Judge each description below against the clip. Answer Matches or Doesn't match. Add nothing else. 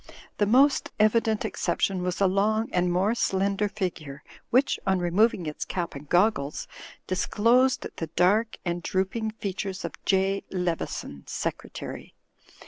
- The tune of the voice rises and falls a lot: Doesn't match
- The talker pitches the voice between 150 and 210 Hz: Matches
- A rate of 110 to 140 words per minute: Matches